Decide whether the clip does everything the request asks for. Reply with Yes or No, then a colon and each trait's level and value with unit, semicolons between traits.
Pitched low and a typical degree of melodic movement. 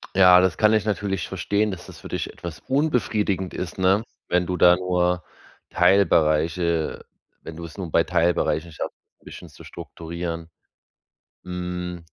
No: very low, 90 Hz; narrow, 2.2 semitones